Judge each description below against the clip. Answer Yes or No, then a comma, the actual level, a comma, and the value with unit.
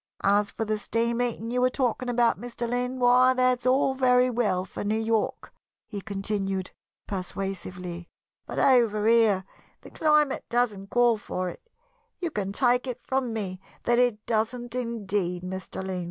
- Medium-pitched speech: No, high, 230 Hz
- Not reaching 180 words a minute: Yes, average, 160 wpm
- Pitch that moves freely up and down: No, average, 3.9 semitones